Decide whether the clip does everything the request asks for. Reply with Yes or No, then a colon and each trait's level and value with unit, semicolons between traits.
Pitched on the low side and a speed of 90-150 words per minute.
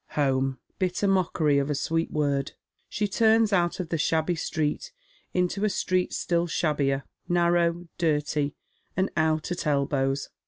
No: medium, 165 Hz; average, 145 wpm